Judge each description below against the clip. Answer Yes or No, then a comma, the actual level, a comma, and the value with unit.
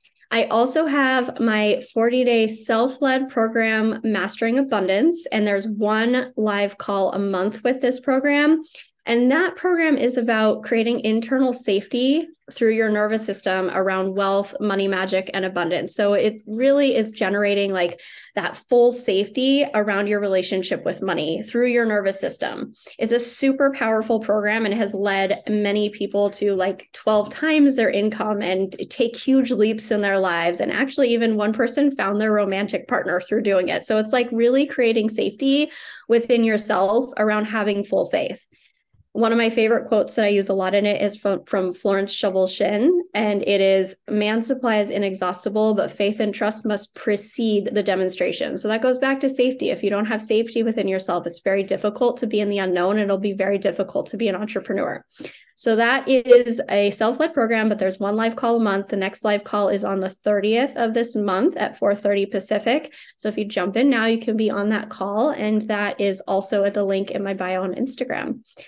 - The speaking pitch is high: Yes, high, 215 Hz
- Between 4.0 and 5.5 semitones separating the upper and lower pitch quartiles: No, average, 3.3 semitones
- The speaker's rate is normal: Yes, average, 190 wpm